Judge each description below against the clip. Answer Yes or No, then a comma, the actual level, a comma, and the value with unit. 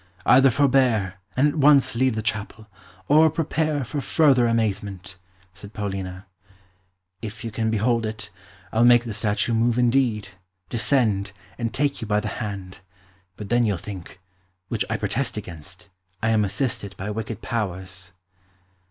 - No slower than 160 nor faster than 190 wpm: No, average, 150 wpm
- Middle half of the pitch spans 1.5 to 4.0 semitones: Yes, average, 3.6 semitones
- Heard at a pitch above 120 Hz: No, low, 110 Hz